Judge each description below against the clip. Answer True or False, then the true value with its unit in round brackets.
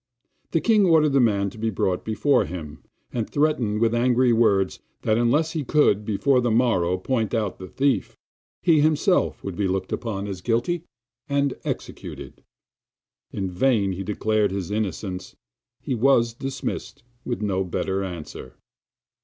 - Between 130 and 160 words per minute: True (155 wpm)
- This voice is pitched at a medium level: False (110 Hz)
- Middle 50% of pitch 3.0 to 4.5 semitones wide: False (5.6 semitones)